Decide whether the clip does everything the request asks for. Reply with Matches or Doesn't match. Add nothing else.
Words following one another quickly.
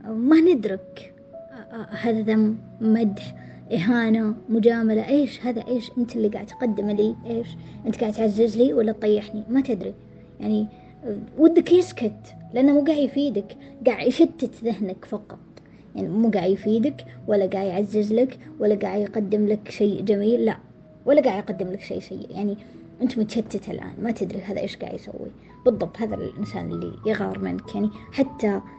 Matches